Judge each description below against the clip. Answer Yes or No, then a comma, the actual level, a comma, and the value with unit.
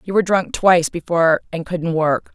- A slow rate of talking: No, fast, 205 wpm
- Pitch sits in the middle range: Yes, medium, 175 Hz